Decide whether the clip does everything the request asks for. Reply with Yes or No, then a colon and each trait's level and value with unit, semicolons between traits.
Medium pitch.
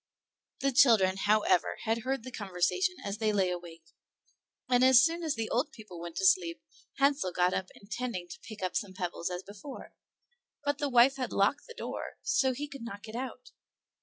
No: high, 225 Hz